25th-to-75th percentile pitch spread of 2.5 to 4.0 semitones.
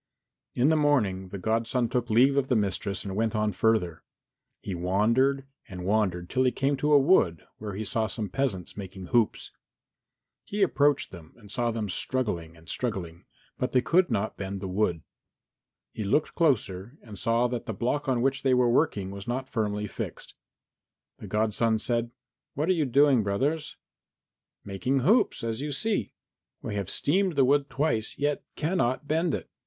No: wide, 5.6 semitones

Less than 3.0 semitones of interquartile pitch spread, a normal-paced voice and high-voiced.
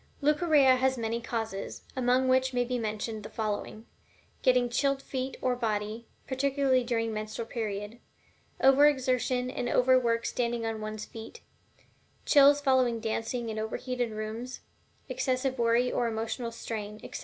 Yes: narrow, 2.6 semitones; average, 145 wpm; high, 240 Hz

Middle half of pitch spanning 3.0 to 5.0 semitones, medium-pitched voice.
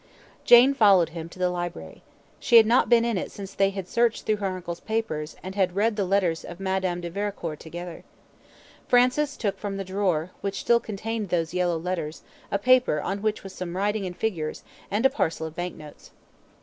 No: average, 3.7 semitones; high, 195 Hz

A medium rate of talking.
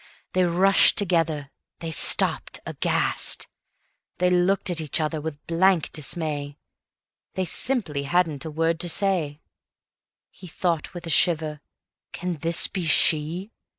No: slow, 130 wpm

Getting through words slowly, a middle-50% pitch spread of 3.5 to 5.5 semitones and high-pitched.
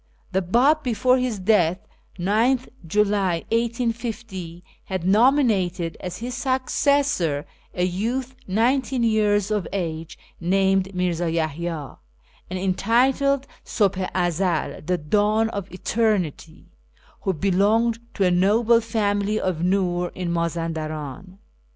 Yes: slow, 115 wpm; average, 4.6 semitones; high, 195 Hz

